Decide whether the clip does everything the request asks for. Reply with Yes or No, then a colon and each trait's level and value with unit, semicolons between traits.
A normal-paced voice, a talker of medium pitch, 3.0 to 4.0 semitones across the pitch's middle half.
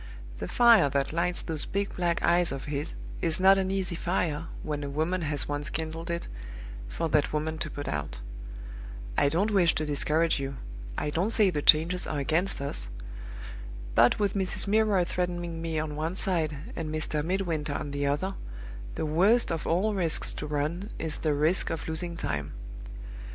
Yes: average, 180 wpm; medium, 160 Hz; average, 3.4 semitones